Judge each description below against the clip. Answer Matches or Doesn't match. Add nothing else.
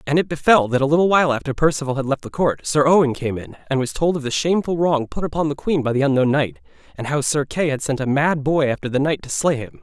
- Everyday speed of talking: Doesn't match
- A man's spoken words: Matches